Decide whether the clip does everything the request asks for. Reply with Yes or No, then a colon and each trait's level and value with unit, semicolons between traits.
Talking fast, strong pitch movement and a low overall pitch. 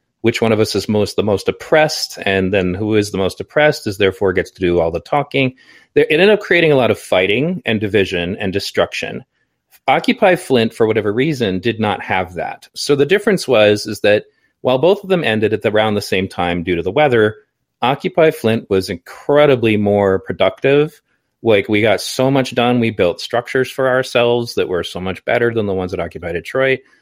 Yes: fast, 210 wpm; wide, 6.0 semitones; low, 115 Hz